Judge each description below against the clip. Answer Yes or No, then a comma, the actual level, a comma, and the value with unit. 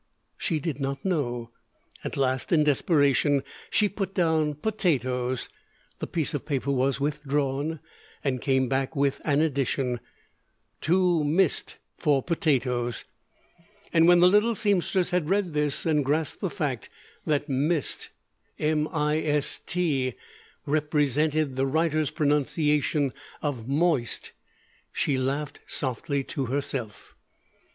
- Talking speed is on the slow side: Yes, slow, 120 wpm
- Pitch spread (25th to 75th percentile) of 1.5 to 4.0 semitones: Yes, average, 3.1 semitones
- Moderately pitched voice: Yes, medium, 150 Hz